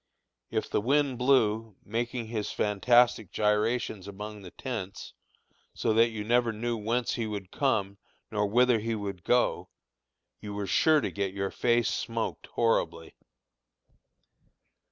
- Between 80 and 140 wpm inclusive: Yes, slow, 135 wpm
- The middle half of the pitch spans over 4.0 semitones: No, average, 2.7 semitones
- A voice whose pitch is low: Yes, low, 110 Hz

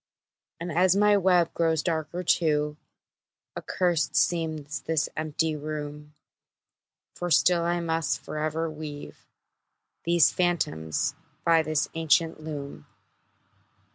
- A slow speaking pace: Yes, slow, 105 wpm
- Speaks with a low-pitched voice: No, medium, 160 Hz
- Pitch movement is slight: Yes, narrow, 2.2 semitones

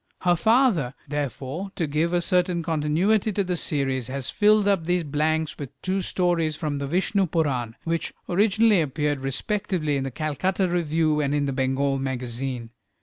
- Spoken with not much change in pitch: No, average, 4.6 semitones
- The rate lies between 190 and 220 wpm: No, average, 160 wpm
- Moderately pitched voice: Yes, medium, 155 Hz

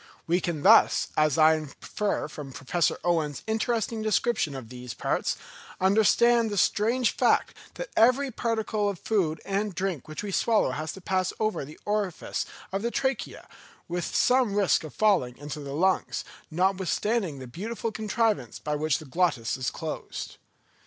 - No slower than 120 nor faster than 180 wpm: Yes, average, 160 wpm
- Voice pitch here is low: No, high, 190 Hz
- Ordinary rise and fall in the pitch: No, wide, 6.0 semitones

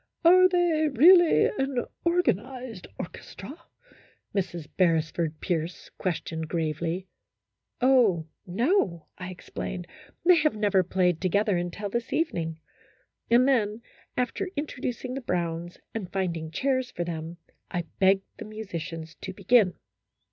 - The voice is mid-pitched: No, high, 195 Hz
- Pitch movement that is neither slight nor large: No, wide, 6.8 semitones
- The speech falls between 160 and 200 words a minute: No, slow, 135 wpm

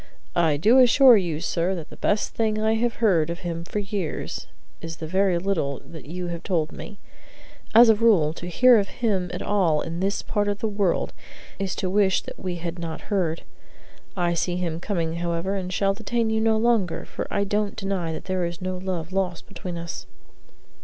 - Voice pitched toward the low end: No, medium, 185 Hz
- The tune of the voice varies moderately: Yes, average, 3.4 semitones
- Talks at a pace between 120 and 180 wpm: No, fast, 205 wpm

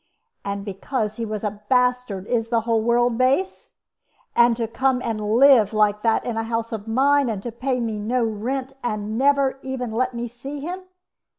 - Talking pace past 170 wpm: Yes, average, 185 wpm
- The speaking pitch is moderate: No, high, 235 Hz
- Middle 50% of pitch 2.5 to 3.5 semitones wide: Yes, average, 2.9 semitones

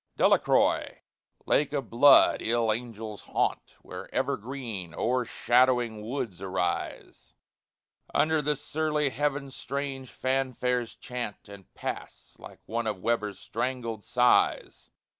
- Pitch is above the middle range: No, low, 125 Hz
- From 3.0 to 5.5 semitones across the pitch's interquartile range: Yes, average, 3.7 semitones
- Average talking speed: No, slow, 110 wpm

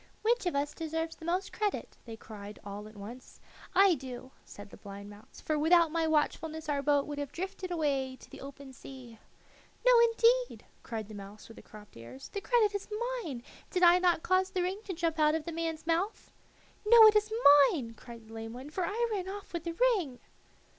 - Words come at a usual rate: No, fast, 210 wpm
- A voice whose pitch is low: No, very high, 315 Hz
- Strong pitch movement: Yes, wide, 7.3 semitones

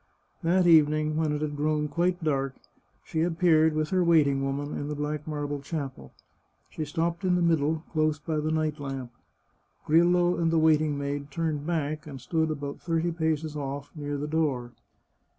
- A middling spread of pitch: No, narrow, 2.1 semitones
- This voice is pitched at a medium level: Yes, medium, 155 Hz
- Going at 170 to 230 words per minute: Yes, average, 180 wpm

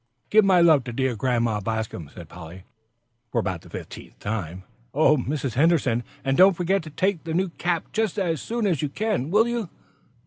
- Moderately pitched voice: Yes, medium, 150 Hz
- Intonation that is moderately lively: No, wide, 8.3 semitones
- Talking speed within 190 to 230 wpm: Yes, average, 200 wpm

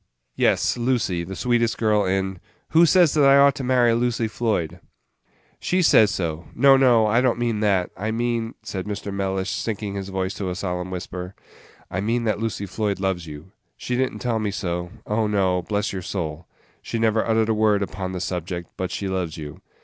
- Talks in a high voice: No, low, 105 Hz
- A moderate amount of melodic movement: Yes, average, 3.8 semitones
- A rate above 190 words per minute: Yes, fast, 205 wpm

